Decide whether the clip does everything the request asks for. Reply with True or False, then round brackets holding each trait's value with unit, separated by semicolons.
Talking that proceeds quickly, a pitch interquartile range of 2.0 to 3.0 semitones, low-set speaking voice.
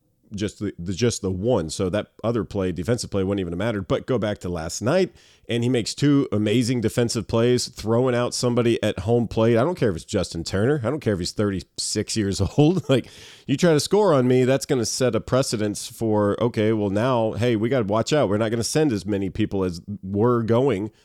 False (240 wpm; 3.6 semitones; 115 Hz)